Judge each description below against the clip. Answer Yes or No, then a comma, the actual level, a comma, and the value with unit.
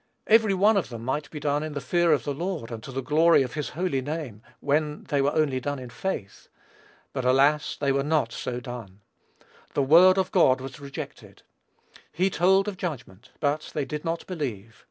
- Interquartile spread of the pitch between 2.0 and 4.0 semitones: No, average, 4.4 semitones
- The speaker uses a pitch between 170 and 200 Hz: No, medium, 145 Hz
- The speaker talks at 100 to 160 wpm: No, average, 195 wpm